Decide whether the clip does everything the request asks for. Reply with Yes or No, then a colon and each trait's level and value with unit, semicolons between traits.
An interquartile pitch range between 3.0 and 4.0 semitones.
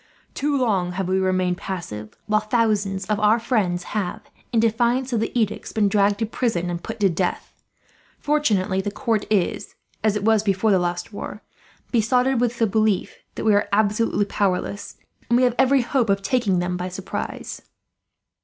Yes: average, 3.4 semitones